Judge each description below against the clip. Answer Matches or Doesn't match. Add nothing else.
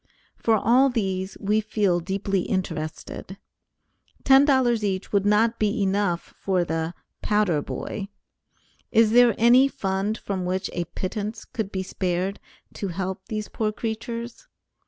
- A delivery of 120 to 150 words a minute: Matches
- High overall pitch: Matches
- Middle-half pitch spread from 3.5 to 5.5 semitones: Doesn't match